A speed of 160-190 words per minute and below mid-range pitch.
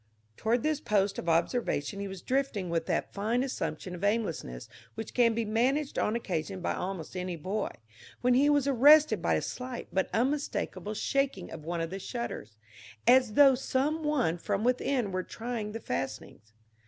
No: average, 175 wpm; high, 225 Hz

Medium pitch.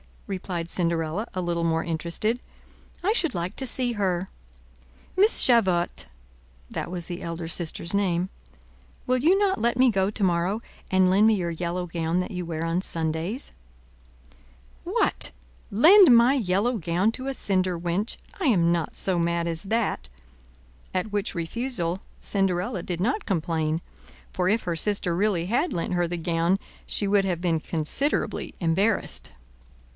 Yes: medium, 180 Hz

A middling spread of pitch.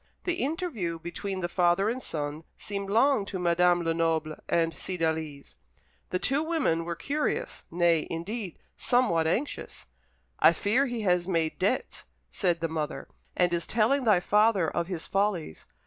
Yes: average, 5.0 semitones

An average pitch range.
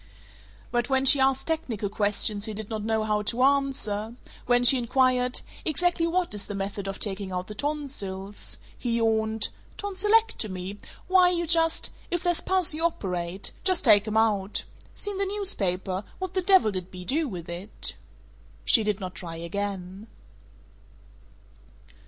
No: wide, 7.8 semitones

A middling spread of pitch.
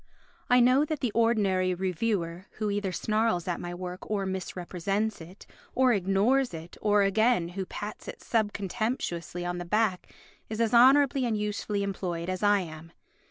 Yes: average, 3.8 semitones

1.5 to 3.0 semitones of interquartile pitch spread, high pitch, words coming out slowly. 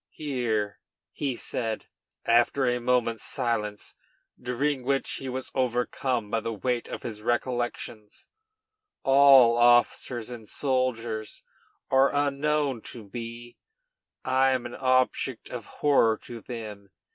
No: narrow, 2.4 semitones; low, 120 Hz; slow, 120 wpm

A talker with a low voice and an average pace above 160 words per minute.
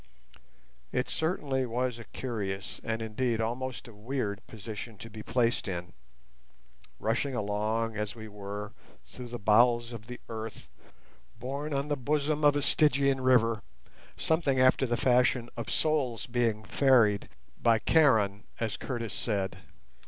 No: low, 115 Hz; slow, 135 wpm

